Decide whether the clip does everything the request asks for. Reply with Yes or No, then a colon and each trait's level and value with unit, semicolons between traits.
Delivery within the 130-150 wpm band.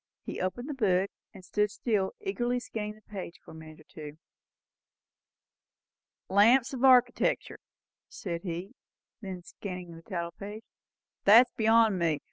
Yes: average, 145 wpm